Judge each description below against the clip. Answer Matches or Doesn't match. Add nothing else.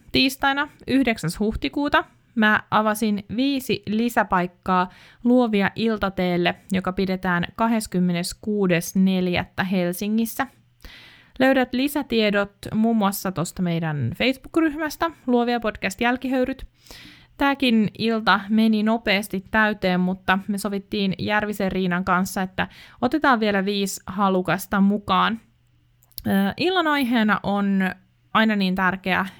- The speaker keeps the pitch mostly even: Doesn't match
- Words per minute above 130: Doesn't match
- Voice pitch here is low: Doesn't match